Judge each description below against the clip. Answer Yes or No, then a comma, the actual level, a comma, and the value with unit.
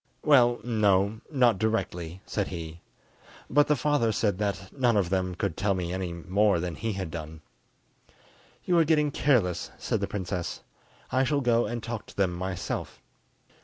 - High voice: No, low, 100 Hz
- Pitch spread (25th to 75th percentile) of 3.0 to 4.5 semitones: No, average, 4.9 semitones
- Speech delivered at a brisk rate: No, average, 165 wpm